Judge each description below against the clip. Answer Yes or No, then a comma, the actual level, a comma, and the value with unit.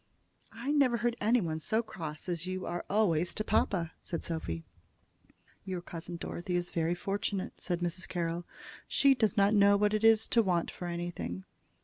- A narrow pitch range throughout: No, average, 3.9 semitones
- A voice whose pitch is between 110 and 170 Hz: No, medium, 180 Hz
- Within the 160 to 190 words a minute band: Yes, average, 170 wpm